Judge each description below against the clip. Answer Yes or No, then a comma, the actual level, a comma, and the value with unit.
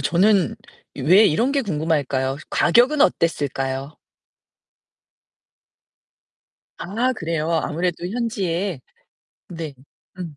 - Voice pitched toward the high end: No, medium, 170 Hz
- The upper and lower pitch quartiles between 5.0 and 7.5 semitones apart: Yes, average, 5.3 semitones